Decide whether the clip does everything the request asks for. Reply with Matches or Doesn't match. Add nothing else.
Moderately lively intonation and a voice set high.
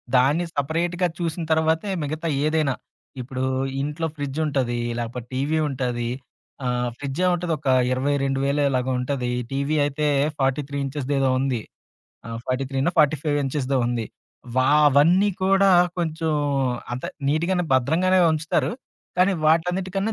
Doesn't match